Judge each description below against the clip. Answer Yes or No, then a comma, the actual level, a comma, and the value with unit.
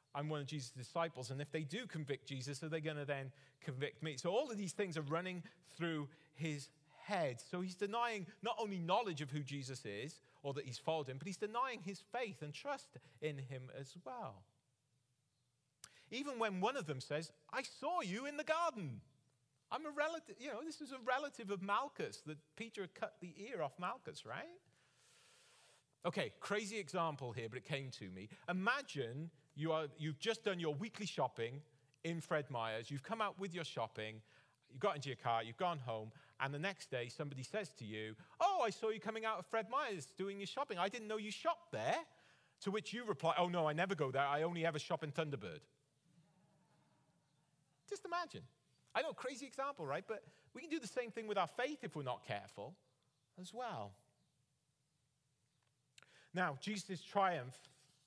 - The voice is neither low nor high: Yes, medium, 160 Hz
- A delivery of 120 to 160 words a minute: No, average, 195 wpm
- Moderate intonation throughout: No, wide, 6.9 semitones